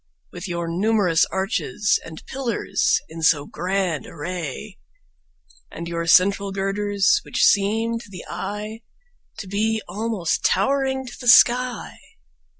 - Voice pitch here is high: Yes, high, 195 Hz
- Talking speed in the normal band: No, slow, 125 wpm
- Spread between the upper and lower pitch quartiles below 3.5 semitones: No, average, 4.3 semitones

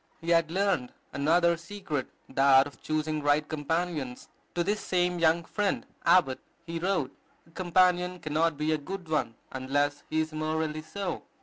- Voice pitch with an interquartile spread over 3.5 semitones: No, average, 3.2 semitones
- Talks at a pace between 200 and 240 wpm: No, average, 160 wpm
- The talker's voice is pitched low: No, medium, 160 Hz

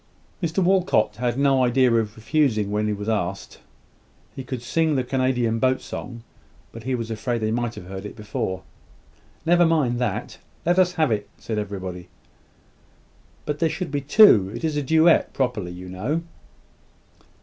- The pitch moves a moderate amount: No, wide, 5.8 semitones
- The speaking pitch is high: No, low, 120 Hz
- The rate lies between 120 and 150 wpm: No, average, 170 wpm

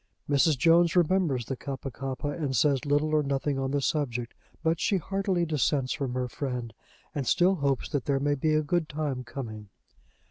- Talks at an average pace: Yes, average, 185 wpm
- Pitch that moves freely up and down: No, average, 2.9 semitones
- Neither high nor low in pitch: Yes, medium, 145 Hz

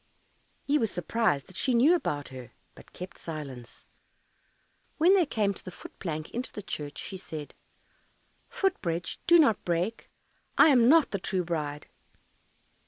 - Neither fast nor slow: Yes, average, 160 wpm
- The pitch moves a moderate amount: No, wide, 8.3 semitones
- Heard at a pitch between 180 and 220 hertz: Yes, medium, 185 Hz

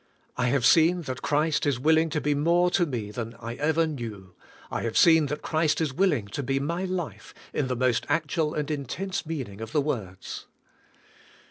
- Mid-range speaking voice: Yes, medium, 150 Hz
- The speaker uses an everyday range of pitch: Yes, average, 4.6 semitones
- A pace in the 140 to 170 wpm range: No, average, 195 wpm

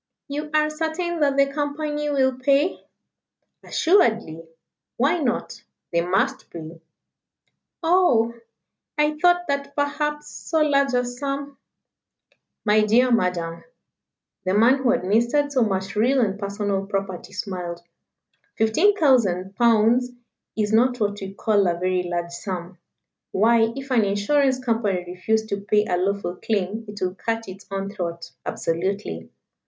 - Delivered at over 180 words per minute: No, average, 140 wpm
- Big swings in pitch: Yes, wide, 6.4 semitones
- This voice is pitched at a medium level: No, high, 225 Hz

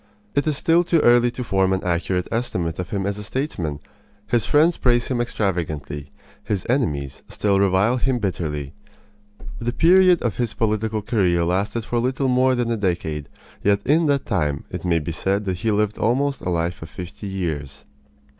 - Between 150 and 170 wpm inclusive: No, average, 185 wpm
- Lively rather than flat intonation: Yes, wide, 5.7 semitones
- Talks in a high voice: No, low, 105 Hz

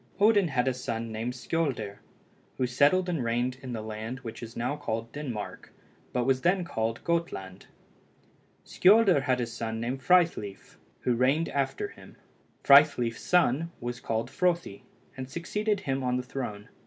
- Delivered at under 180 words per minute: Yes, average, 155 wpm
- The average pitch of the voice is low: Yes, low, 130 Hz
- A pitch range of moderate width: No, wide, 6.1 semitones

